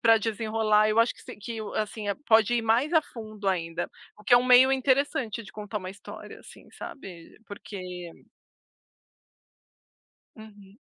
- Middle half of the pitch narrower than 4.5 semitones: Yes, narrow, 2.4 semitones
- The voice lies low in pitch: No, high, 215 Hz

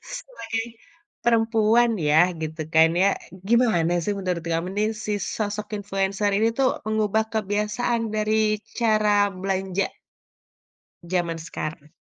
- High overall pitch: Yes, high, 205 Hz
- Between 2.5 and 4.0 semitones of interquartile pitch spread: Yes, average, 3.3 semitones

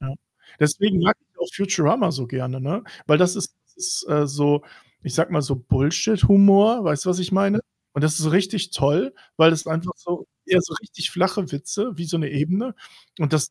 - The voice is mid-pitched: Yes, medium, 170 Hz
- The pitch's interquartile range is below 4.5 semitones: No, average, 4.9 semitones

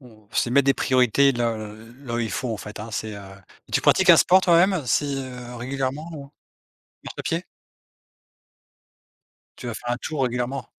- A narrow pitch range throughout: No, average, 3.1 semitones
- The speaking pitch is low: Yes, low, 125 Hz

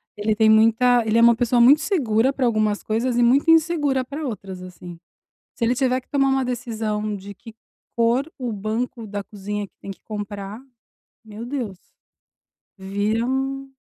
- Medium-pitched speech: No, high, 230 Hz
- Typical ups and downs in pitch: Yes, average, 3.5 semitones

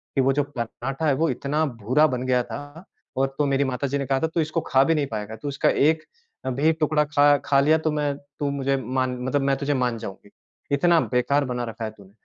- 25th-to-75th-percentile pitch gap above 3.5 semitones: No, average, 2.9 semitones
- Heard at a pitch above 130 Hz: Yes, medium, 140 Hz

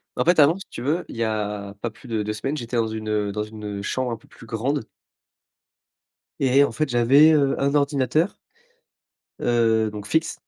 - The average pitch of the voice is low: Yes, low, 120 Hz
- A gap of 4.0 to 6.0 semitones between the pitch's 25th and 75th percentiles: Yes, average, 4.7 semitones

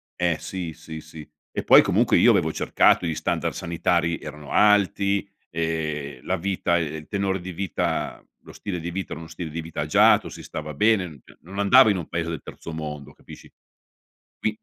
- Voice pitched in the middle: No, very low, 85 Hz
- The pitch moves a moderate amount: Yes, average, 3.3 semitones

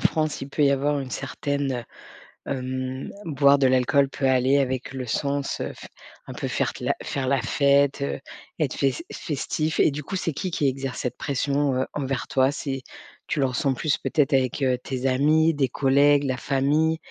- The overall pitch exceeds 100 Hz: Yes, medium, 140 Hz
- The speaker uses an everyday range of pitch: No, narrow, 1.7 semitones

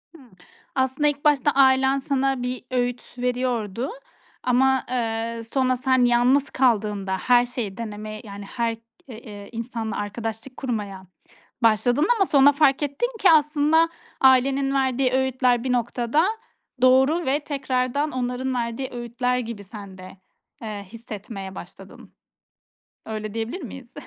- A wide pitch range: No, average, 2.9 semitones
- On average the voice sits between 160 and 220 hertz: No, very high, 250 Hz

